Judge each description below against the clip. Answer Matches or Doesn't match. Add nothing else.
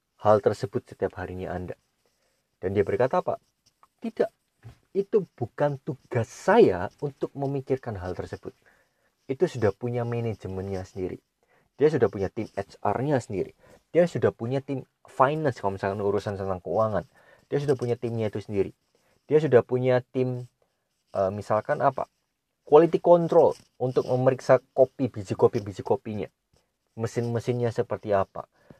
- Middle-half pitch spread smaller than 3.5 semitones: Doesn't match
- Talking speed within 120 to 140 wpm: Matches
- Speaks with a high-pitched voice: Doesn't match